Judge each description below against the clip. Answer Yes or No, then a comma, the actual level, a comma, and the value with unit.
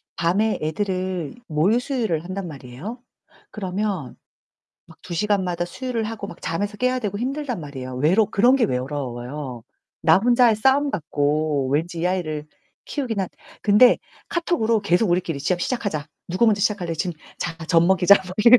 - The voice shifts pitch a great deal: Yes, wide, 6.0 semitones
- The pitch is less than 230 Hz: Yes, medium, 185 Hz